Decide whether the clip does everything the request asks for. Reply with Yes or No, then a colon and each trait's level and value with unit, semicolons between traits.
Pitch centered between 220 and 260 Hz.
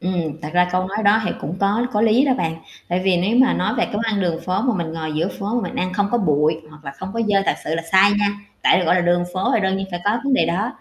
No: high, 190 Hz